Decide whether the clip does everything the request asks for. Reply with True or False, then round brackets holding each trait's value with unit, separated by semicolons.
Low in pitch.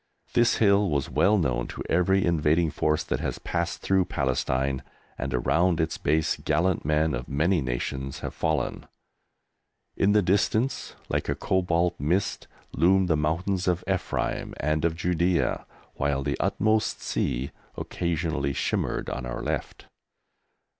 True (80 Hz)